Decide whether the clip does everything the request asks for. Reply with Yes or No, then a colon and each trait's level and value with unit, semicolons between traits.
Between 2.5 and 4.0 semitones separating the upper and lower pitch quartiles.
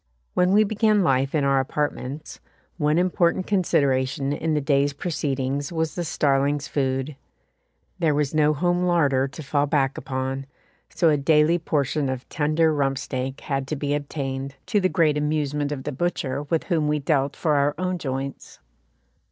Yes: average, 2.9 semitones